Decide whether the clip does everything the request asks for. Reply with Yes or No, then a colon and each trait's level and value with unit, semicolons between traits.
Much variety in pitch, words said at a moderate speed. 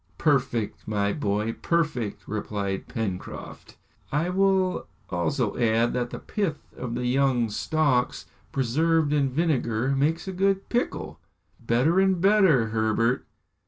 No: wide, 6.5 semitones; slow, 125 wpm